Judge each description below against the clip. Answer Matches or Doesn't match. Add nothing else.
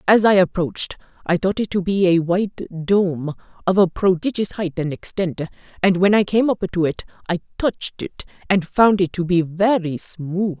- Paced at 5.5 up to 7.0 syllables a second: Doesn't match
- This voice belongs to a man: Doesn't match